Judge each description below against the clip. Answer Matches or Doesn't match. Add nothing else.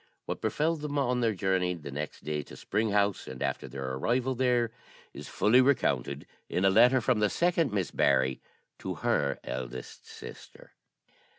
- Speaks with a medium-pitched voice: Doesn't match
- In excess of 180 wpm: Doesn't match